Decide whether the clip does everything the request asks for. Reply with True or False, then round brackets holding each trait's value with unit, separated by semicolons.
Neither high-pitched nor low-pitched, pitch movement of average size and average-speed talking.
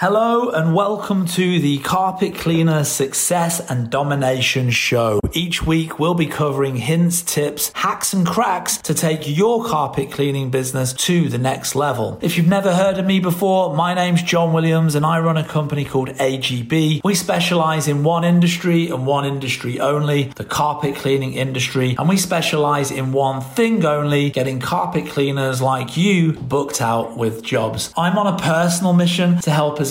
True (155 Hz; 4.2 semitones; 175 wpm)